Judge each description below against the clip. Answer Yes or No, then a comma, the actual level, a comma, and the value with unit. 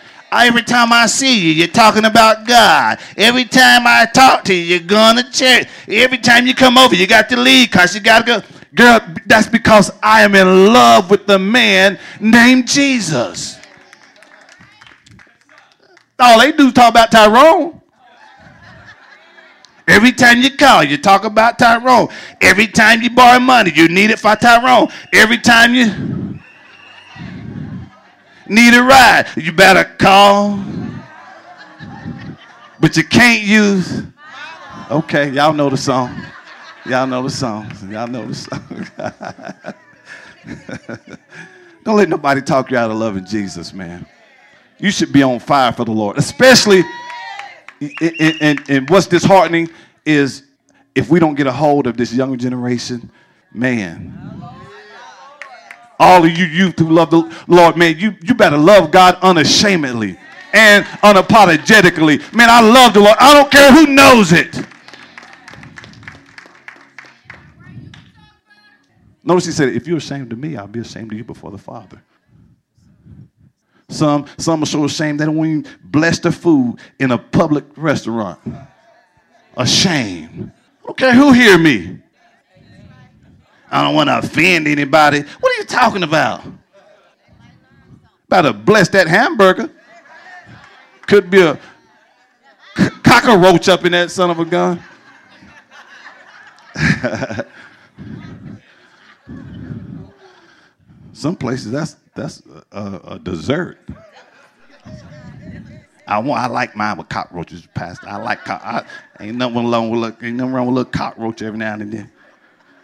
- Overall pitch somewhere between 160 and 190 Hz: Yes, medium, 185 Hz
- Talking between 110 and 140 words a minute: Yes, slow, 135 wpm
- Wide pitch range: Yes, wide, 8.5 semitones